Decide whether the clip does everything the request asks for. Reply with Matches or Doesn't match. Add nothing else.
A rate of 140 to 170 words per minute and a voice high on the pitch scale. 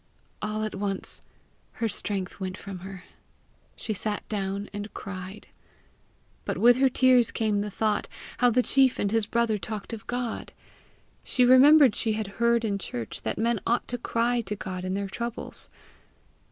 Matches